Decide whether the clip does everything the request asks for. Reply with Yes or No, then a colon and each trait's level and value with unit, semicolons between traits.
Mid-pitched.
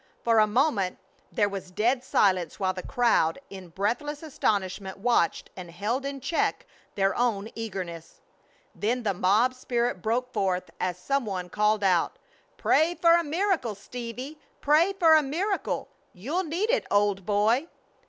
No: high, 225 Hz